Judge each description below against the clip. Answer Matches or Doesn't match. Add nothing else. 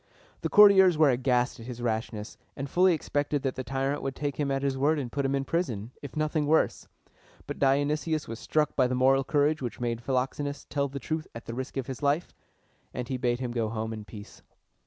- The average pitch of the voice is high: Doesn't match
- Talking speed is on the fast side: Matches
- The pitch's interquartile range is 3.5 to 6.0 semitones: Doesn't match